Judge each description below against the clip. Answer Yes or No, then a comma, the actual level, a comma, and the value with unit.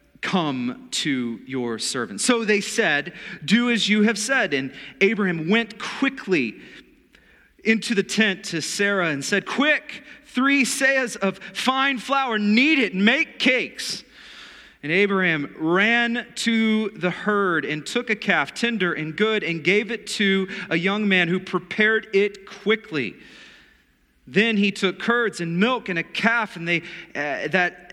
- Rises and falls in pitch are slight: No, average, 4.5 semitones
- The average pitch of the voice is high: Yes, high, 210 Hz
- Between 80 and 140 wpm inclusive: No, average, 155 wpm